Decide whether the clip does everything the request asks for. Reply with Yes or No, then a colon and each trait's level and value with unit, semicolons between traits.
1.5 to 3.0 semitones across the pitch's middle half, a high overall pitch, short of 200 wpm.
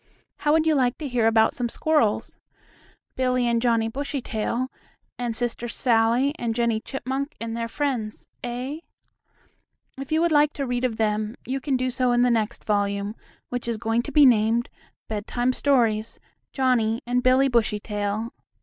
Yes: narrow, 2.6 semitones; high, 240 Hz; average, 165 wpm